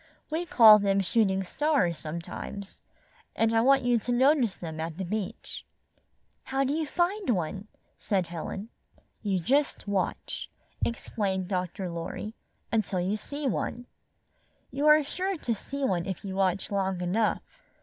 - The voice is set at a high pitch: Yes, high, 210 Hz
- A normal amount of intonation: No, wide, 6.1 semitones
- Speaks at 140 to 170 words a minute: Yes, average, 150 wpm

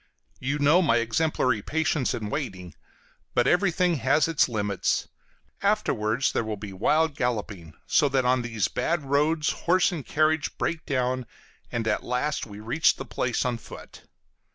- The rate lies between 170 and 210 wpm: No, average, 155 wpm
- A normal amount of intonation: No, wide, 5.7 semitones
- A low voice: Yes, low, 130 Hz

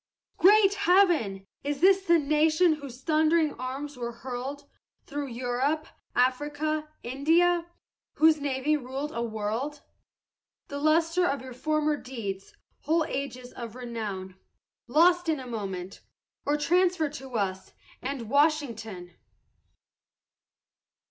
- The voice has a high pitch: Yes, very high, 285 Hz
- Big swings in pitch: No, average, 4.3 semitones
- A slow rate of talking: Yes, slow, 115 wpm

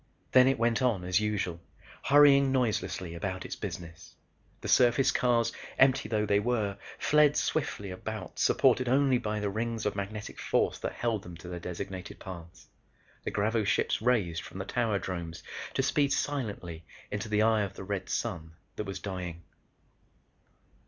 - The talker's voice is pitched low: Yes, low, 105 Hz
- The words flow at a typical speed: Yes, average, 160 wpm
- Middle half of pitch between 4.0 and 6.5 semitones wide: Yes, average, 4.8 semitones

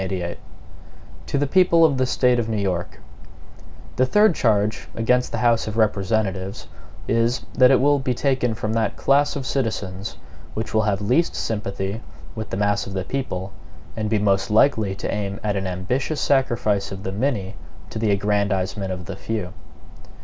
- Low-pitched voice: Yes, low, 110 Hz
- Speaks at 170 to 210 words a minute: Yes, average, 175 wpm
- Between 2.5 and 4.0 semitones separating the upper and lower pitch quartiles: No, average, 4.4 semitones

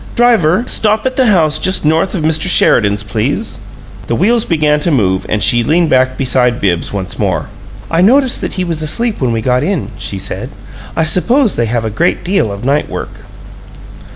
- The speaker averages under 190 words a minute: No, average, 195 wpm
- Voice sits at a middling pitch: Yes, medium, 155 Hz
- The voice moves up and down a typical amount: No, wide, 8.2 semitones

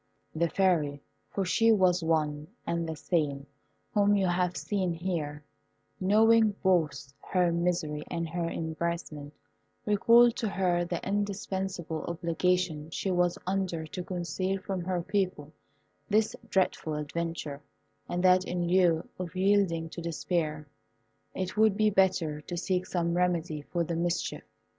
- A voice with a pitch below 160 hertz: No, medium, 175 Hz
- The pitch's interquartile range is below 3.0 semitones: Yes, narrow, 2.6 semitones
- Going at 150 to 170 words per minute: No, average, 140 wpm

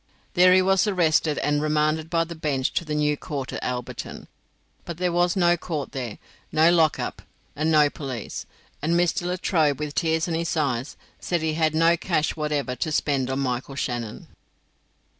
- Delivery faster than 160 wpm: Yes, average, 180 wpm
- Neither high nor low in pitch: Yes, medium, 155 Hz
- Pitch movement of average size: Yes, average, 3.0 semitones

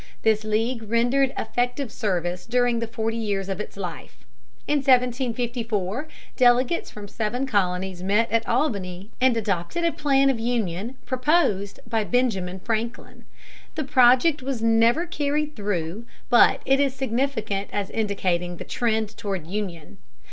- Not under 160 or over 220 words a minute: No, average, 140 wpm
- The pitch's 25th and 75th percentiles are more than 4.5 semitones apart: No, average, 4.1 semitones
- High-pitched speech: Yes, high, 230 Hz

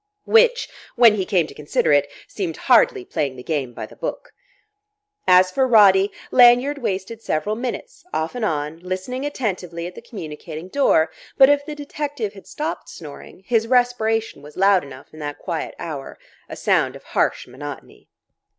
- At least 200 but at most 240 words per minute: No, average, 170 wpm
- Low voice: No, high, 195 Hz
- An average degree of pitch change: No, wide, 7.7 semitones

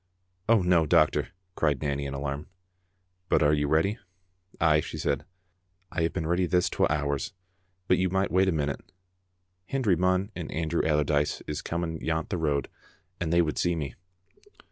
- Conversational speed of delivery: Yes, average, 180 wpm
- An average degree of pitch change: Yes, average, 3.5 semitones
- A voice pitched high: No, very low, 80 Hz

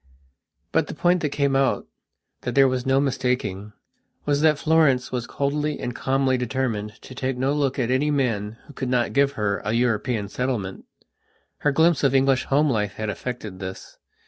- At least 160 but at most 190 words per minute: Yes, average, 170 wpm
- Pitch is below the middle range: Yes, low, 130 Hz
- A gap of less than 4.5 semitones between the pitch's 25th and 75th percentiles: Yes, average, 3.3 semitones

